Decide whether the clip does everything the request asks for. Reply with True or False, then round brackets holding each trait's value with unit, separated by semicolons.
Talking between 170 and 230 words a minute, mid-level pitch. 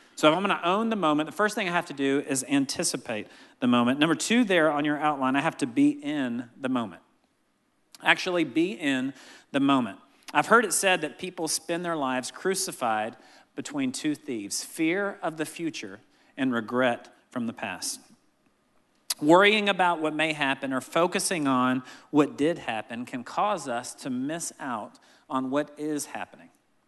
True (180 wpm; 160 Hz)